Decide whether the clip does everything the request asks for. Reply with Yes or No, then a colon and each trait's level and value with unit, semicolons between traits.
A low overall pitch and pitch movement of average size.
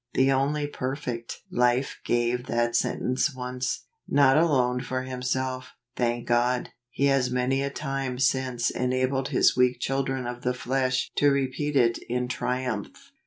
No: low, 130 Hz; narrow, 1.4 semitones